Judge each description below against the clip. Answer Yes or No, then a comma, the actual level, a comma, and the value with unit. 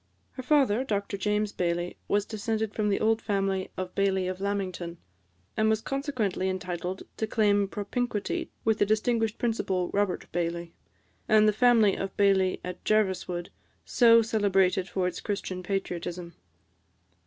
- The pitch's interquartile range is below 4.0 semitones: Yes, average, 2.8 semitones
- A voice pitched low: No, high, 200 Hz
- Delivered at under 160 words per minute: Yes, average, 140 wpm